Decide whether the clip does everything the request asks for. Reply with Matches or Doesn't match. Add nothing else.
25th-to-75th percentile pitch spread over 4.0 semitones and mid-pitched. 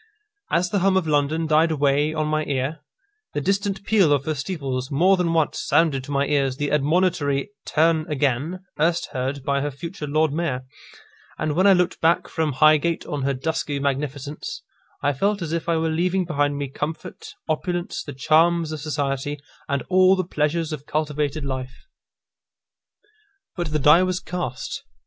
Doesn't match